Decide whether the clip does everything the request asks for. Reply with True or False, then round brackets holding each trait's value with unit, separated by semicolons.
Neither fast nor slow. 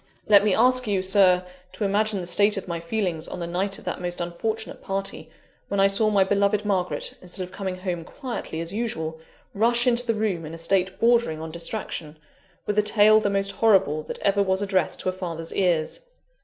False (210 wpm)